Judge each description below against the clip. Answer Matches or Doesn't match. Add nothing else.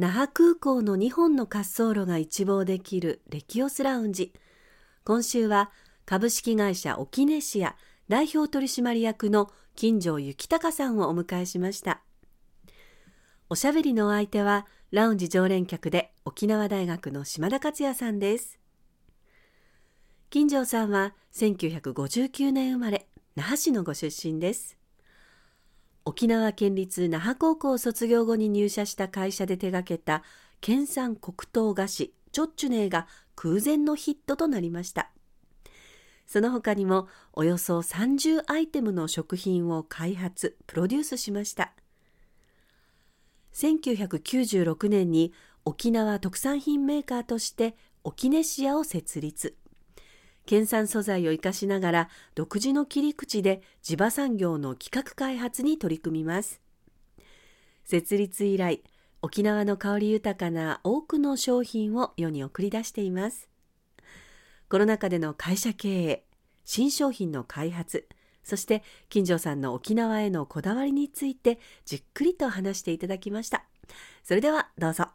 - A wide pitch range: Matches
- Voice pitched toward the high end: Matches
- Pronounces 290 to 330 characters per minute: Doesn't match